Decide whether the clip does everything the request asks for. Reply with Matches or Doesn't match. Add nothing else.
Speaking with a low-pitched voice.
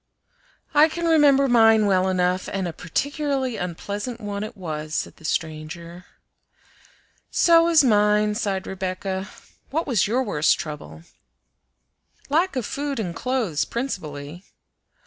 Doesn't match